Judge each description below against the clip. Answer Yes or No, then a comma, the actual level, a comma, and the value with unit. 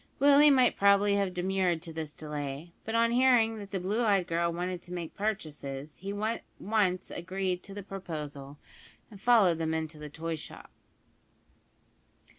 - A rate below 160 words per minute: No, average, 165 wpm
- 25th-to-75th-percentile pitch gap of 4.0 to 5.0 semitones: Yes, average, 4.3 semitones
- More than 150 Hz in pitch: Yes, medium, 185 Hz